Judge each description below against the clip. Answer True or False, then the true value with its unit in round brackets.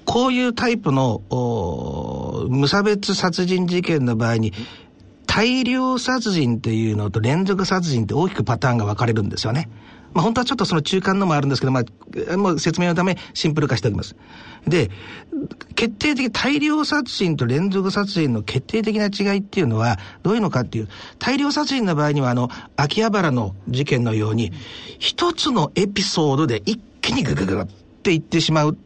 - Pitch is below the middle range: False (160 Hz)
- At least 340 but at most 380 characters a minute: True (360 characters per minute)